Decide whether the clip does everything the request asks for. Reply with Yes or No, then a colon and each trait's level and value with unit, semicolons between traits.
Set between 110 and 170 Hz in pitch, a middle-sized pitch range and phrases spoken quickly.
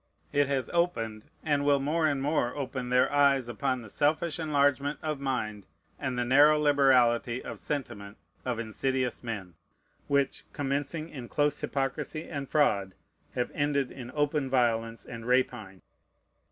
No: low, 135 Hz; average, 3.3 semitones; average, 145 wpm